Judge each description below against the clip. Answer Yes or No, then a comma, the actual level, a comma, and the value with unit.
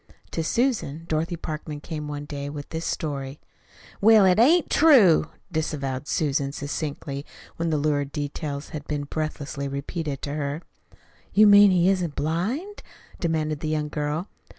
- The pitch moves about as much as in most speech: Yes, average, 3.2 semitones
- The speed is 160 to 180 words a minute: No, average, 150 wpm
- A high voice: No, medium, 155 Hz